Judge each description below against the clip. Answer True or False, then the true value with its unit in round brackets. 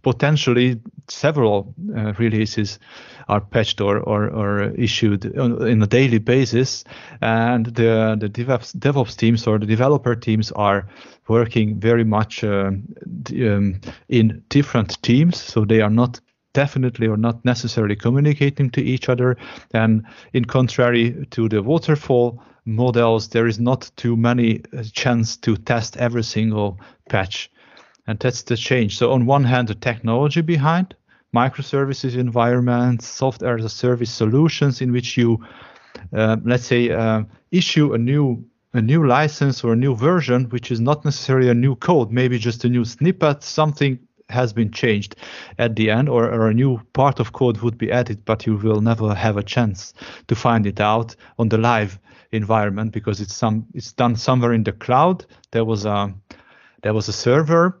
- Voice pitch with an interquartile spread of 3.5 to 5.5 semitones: False (2.6 semitones)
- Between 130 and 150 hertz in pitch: False (120 Hz)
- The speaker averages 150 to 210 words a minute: True (165 wpm)